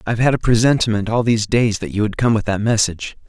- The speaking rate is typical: No, fast, 255 wpm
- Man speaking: Yes, male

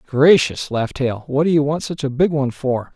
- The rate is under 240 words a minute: No, fast, 245 wpm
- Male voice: Yes, male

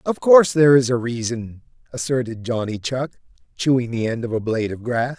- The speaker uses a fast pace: No, average, 195 wpm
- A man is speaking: Yes, male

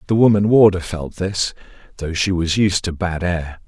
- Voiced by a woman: No, male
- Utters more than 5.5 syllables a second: No, 4.7 syllables/s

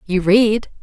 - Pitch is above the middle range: Yes, high, 205 Hz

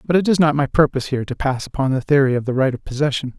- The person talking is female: No, male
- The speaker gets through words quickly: Yes, fast, 300 wpm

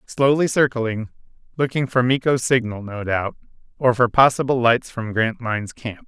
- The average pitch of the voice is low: Yes, low, 120 Hz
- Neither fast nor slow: Yes, average, 150 wpm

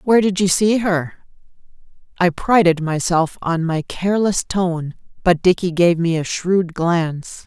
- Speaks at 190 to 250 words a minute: No, average, 155 wpm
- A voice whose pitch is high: No, medium, 175 Hz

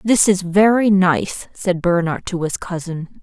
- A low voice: No, medium, 185 Hz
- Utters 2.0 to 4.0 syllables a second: Yes, 3.9 syllables/s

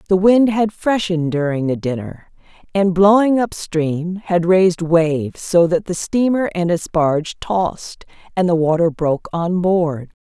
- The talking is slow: No, average, 165 wpm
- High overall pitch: No, medium, 175 Hz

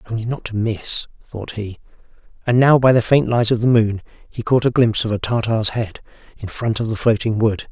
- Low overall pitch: Yes, low, 115 Hz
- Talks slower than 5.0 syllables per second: No, 5.4 syllables/s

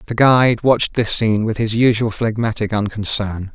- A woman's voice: No, male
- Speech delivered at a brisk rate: No, average, 170 wpm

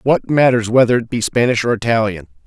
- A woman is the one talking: No, male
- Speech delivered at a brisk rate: No, average, 195 wpm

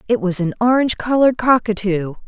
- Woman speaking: Yes, female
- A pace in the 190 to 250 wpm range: No, average, 160 wpm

